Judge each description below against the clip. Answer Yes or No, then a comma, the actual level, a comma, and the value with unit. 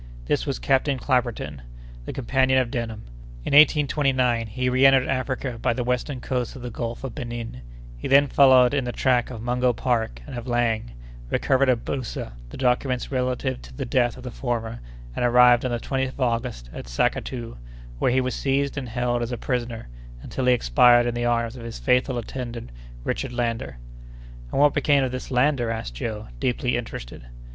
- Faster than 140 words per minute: Yes, average, 185 wpm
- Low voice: Yes, low, 125 Hz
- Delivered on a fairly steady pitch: Yes, narrow, 1.9 semitones